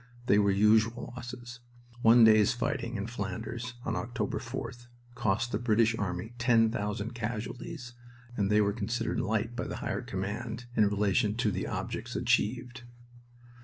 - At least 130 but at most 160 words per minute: Yes, average, 150 wpm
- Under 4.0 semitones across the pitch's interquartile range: Yes, narrow, 2.4 semitones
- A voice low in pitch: Yes, low, 115 Hz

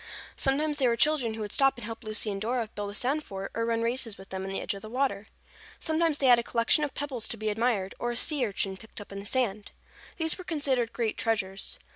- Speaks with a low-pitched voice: No, high, 230 Hz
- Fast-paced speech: Yes, fast, 255 wpm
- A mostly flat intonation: No, average, 4.5 semitones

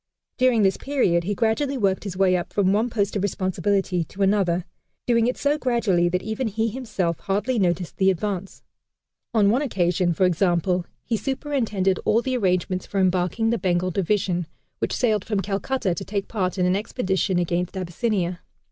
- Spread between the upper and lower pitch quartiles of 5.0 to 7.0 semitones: No, average, 3.6 semitones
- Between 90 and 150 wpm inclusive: No, average, 175 wpm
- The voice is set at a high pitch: Yes, high, 195 Hz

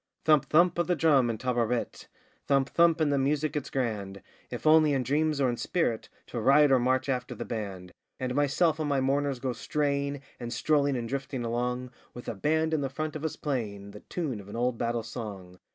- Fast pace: Yes, fast, 220 wpm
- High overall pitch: No, low, 135 Hz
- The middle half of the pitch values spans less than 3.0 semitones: No, average, 3.9 semitones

